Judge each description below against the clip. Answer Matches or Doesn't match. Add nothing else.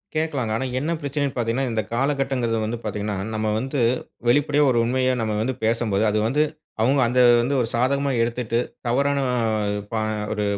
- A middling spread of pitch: Matches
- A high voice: Doesn't match